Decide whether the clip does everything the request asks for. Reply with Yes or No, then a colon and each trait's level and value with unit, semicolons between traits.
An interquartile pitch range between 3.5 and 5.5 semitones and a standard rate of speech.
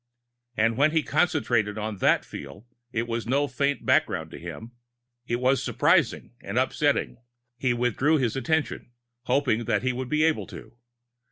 Yes: average, 3.8 semitones; average, 160 wpm